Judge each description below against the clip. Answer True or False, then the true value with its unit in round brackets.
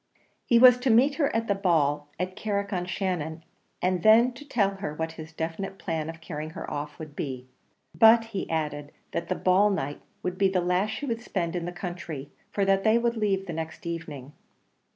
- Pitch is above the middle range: False (180 Hz)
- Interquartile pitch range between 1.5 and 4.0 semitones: False (4.6 semitones)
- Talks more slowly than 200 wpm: False (205 wpm)